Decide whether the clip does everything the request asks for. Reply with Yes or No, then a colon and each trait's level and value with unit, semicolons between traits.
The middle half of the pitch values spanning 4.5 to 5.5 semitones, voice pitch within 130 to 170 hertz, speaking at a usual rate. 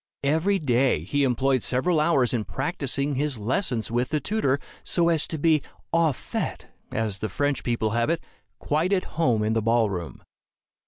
Yes: average, 5.1 semitones; low, 135 Hz; average, 175 wpm